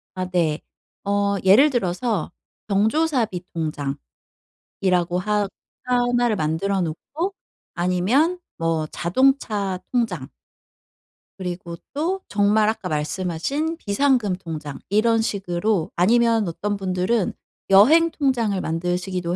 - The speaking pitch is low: No, high, 200 Hz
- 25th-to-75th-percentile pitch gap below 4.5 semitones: No, average, 5.2 semitones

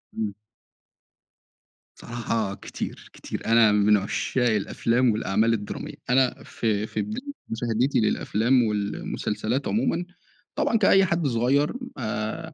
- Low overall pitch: Yes, low, 115 Hz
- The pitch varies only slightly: No, average, 3.7 semitones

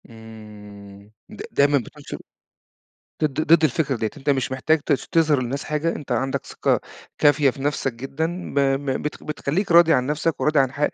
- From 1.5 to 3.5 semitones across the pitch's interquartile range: Yes, average, 3.2 semitones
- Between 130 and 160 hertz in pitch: Yes, medium, 140 Hz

